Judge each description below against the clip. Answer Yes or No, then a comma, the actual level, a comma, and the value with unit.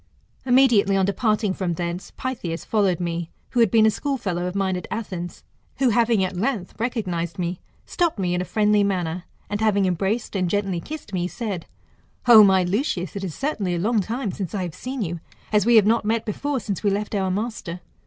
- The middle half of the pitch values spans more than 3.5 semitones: Yes, average, 3.9 semitones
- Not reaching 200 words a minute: No, fast, 205 wpm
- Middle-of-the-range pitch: No, high, 200 Hz